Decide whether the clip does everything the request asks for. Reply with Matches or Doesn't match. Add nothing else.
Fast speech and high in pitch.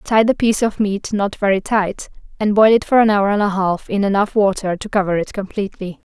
Matches